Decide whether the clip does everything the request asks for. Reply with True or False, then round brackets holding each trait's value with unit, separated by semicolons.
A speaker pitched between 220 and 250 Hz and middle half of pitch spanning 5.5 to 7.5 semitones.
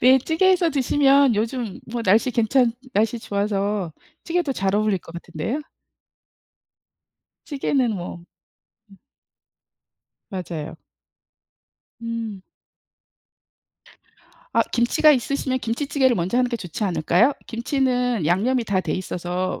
False (230 Hz; 5.1 semitones)